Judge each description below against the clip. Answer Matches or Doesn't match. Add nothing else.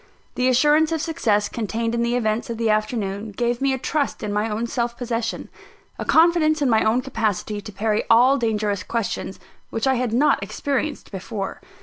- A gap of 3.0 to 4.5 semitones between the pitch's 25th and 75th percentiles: Matches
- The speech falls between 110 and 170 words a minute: Doesn't match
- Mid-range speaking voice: Doesn't match